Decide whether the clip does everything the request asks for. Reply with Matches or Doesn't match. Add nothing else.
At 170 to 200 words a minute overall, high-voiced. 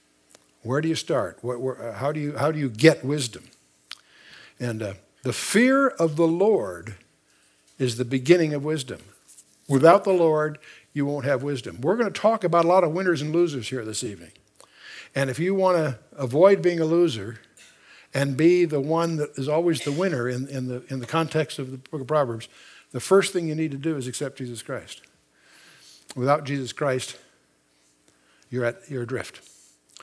Doesn't match